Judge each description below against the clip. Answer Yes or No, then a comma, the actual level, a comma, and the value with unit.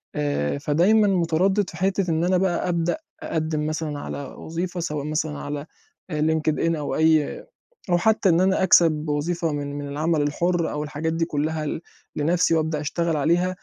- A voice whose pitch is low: No, medium, 160 Hz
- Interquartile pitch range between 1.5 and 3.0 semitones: Yes, average, 2.7 semitones